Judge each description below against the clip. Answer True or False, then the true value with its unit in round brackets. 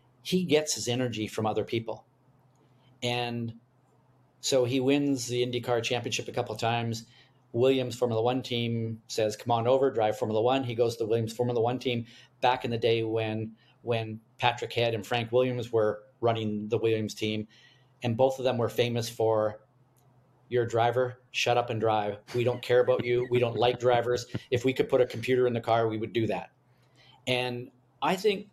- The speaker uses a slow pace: False (195 wpm)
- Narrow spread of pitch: True (1.9 semitones)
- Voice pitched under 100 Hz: False (120 Hz)